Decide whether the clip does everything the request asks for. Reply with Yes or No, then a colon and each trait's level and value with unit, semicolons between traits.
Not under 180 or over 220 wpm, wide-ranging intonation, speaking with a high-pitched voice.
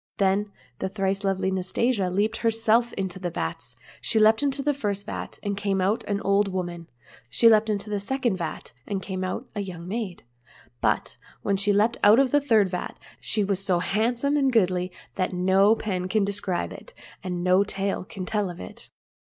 No: average, 195 wpm; average, 2.9 semitones; high, 200 Hz